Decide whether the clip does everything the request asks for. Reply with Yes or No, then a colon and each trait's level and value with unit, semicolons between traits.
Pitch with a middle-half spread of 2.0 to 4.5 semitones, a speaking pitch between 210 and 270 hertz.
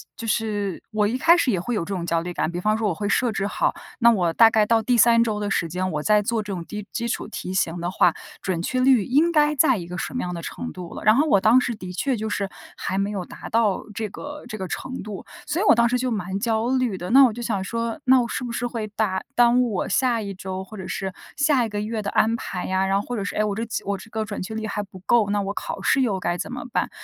Yes: average, 3.7 semitones; high, 215 Hz